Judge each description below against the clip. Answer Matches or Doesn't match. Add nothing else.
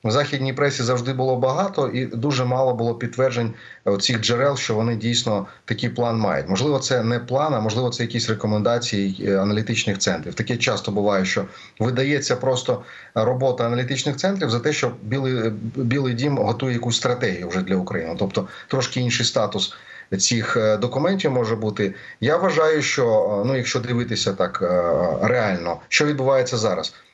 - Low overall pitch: Matches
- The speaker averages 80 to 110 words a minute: Doesn't match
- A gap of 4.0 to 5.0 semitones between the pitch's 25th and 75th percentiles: Doesn't match